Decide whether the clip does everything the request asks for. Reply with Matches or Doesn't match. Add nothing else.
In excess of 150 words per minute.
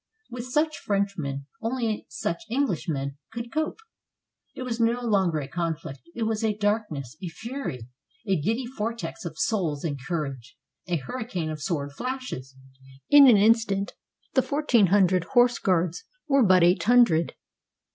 Doesn't match